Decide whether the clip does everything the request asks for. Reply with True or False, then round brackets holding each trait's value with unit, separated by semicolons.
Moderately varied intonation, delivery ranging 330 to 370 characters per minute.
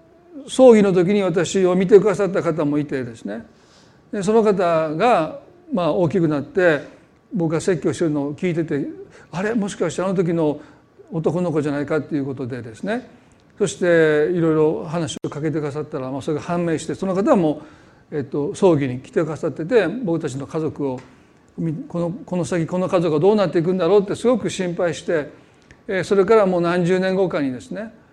True (4.2 semitones; 360 characters per minute)